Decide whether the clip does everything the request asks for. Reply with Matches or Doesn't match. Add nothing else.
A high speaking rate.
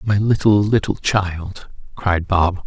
Doesn't match